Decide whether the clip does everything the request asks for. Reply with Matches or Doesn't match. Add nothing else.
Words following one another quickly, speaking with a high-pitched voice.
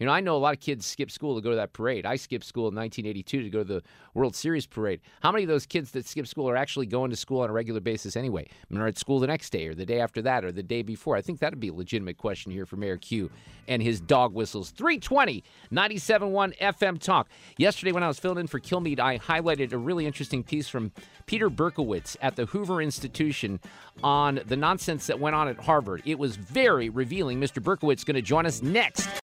Doesn't match